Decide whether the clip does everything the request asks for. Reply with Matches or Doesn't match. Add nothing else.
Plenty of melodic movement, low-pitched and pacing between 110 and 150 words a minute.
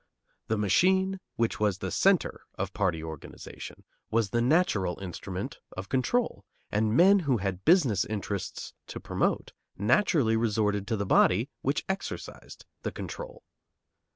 Matches